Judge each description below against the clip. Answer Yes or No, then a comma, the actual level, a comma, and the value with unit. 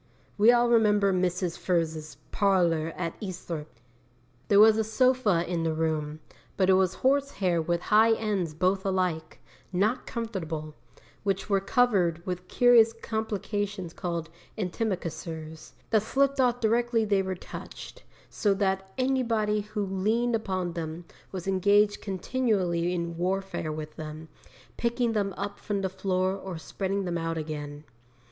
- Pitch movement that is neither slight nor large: Yes, average, 4.2 semitones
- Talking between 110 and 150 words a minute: Yes, average, 140 wpm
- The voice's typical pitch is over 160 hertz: Yes, high, 190 Hz